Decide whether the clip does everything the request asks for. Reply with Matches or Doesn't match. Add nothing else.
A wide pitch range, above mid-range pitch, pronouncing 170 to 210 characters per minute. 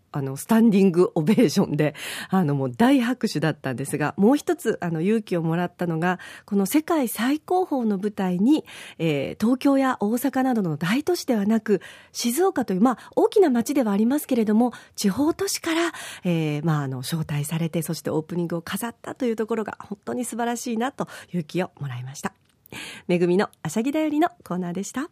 Doesn't match